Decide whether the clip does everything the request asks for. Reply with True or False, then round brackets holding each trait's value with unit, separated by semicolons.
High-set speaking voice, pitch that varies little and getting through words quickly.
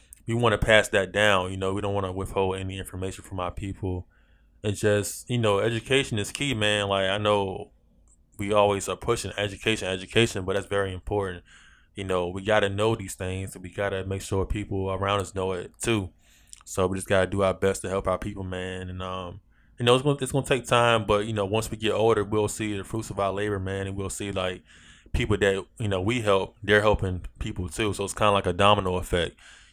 False (100 Hz; 2.0 semitones; 235 wpm)